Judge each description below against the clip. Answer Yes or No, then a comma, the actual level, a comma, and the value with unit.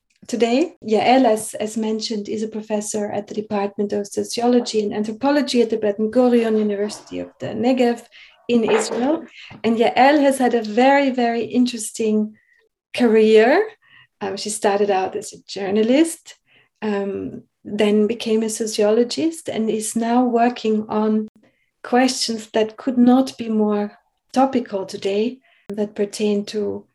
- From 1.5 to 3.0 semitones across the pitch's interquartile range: Yes, narrow, 2.6 semitones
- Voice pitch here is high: Yes, high, 220 Hz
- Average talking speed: Yes, average, 135 wpm